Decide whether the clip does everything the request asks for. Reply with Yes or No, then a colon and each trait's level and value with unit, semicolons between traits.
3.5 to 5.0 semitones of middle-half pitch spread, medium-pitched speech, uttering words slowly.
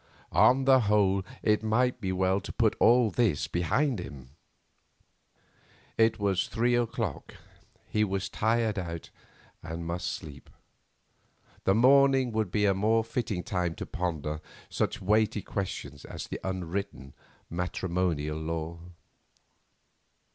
No: average, 4.6 semitones; very low, 95 Hz; slow, 125 wpm